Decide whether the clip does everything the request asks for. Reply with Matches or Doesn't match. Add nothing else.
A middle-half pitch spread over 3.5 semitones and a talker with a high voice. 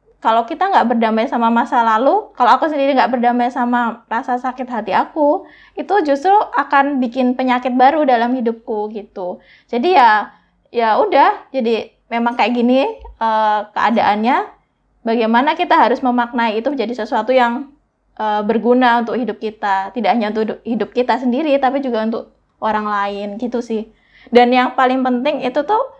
Doesn't match